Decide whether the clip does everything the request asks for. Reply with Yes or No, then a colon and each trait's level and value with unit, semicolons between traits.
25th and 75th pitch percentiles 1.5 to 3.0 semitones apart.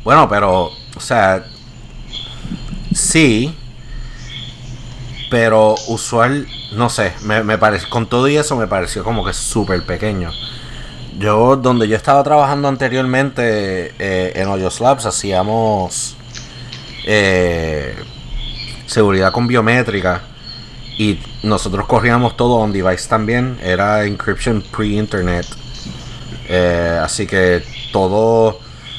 No: average, 3.7 semitones